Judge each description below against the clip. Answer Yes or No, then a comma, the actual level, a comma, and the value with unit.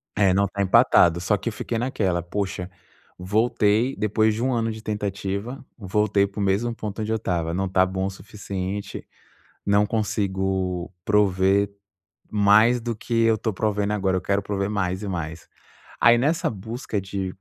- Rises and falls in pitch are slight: Yes, narrow, 2.3 semitones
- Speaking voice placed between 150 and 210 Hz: No, low, 100 Hz